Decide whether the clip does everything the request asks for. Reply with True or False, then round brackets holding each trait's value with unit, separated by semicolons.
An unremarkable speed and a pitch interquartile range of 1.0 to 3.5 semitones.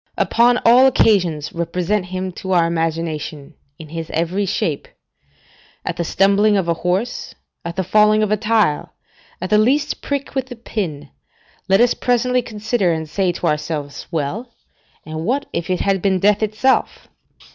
False (165 wpm; 4.6 semitones)